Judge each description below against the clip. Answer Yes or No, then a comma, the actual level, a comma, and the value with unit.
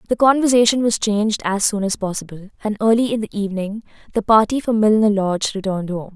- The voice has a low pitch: No, high, 210 Hz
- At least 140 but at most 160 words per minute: No, average, 195 wpm